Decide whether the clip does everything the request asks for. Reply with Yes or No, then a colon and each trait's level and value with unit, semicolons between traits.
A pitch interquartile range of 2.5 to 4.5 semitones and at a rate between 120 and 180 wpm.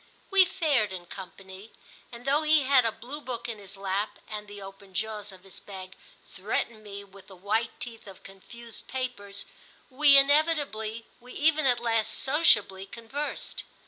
No: average, 5.1 semitones; average, 165 wpm